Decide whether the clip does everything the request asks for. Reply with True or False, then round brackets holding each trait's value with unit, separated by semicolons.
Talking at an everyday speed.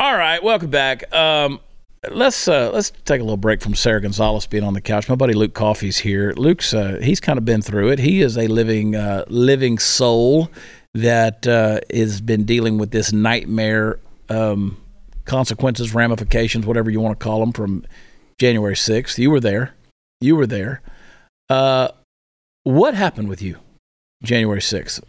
True (170 wpm)